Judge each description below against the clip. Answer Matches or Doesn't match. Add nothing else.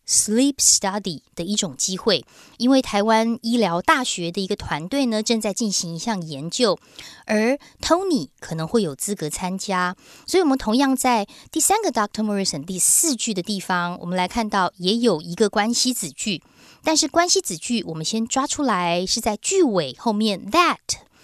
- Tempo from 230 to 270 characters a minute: Doesn't match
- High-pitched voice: Matches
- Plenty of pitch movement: Matches